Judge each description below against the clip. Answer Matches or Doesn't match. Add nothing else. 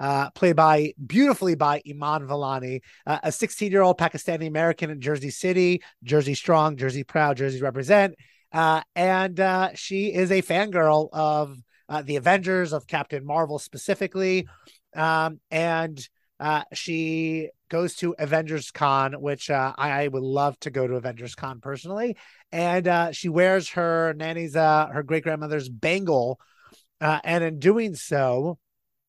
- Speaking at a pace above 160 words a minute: Doesn't match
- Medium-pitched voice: Matches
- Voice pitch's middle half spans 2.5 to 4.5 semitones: Matches